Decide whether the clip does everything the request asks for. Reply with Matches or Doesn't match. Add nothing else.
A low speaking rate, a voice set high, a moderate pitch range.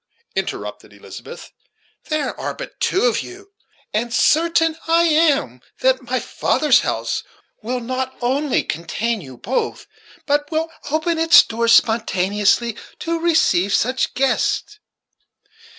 Doesn't match